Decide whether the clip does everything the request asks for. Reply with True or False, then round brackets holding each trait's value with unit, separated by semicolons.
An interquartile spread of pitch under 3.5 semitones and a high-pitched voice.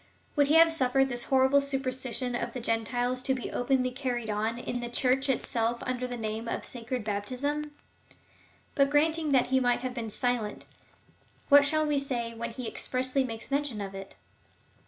True (2.6 semitones; 255 Hz)